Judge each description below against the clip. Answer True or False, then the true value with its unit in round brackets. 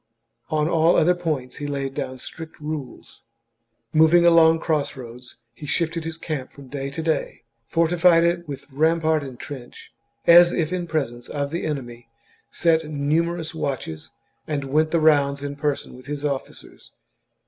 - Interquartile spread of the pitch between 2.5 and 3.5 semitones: True (2.9 semitones)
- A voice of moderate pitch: True (155 Hz)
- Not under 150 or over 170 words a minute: True (160 wpm)